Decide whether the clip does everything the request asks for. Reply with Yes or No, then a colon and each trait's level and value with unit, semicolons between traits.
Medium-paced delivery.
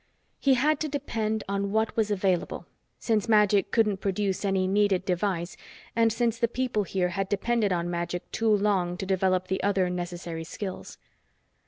Yes: average, 165 wpm